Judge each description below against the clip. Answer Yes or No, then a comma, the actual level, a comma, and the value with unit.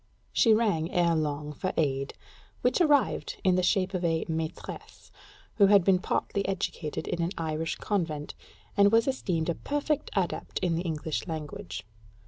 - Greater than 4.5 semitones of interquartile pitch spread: No, average, 4.0 semitones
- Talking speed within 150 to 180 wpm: Yes, average, 160 wpm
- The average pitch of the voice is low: No, medium, 175 Hz